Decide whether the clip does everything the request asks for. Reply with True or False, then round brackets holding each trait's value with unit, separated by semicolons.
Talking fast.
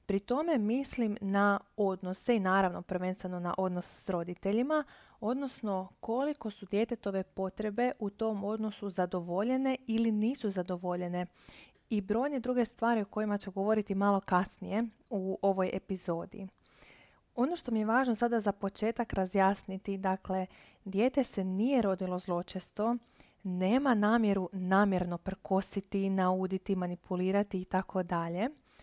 False (125 wpm)